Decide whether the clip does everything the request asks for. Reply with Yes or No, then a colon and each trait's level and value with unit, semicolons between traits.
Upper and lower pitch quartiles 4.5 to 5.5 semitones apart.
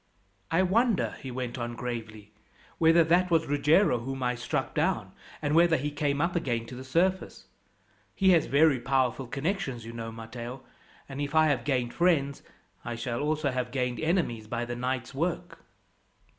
Yes: average, 5.0 semitones